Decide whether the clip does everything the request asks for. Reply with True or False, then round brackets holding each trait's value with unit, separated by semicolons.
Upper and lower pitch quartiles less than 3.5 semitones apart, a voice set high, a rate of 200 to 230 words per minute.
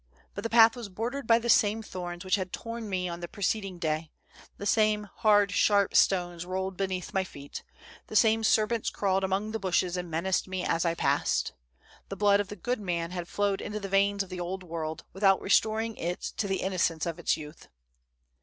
True (3.1 semitones; 195 Hz; 205 wpm)